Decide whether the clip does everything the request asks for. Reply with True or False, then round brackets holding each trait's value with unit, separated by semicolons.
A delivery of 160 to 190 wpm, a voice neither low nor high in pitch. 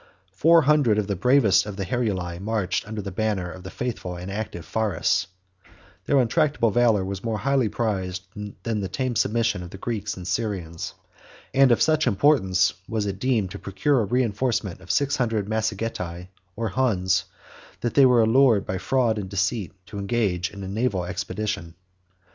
False (175 wpm; 105 Hz)